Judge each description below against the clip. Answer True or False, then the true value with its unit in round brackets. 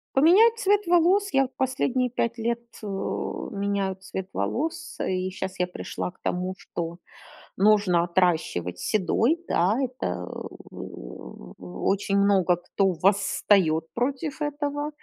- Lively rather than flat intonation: True (6.9 semitones)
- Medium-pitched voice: False (200 Hz)